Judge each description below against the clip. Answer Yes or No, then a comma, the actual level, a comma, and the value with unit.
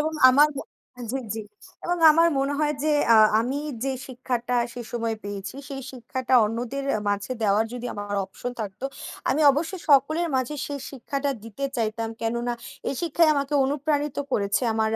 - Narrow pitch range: No, average, 4.2 semitones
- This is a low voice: No, very high, 260 Hz